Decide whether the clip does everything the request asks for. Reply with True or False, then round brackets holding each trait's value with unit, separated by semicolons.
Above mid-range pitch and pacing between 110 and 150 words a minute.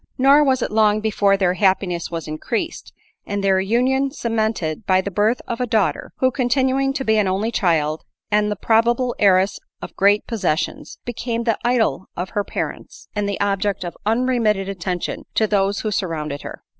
False (210 Hz; 180 wpm)